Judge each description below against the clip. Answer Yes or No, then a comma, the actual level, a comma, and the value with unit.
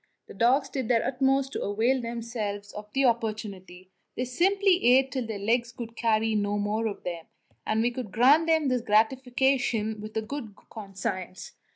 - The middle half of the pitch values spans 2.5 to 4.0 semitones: Yes, average, 3.7 semitones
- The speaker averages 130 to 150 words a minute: No, average, 170 wpm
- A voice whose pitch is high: Yes, high, 230 Hz